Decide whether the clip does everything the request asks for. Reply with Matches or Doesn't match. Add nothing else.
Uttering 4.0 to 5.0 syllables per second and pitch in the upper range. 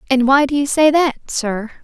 Matches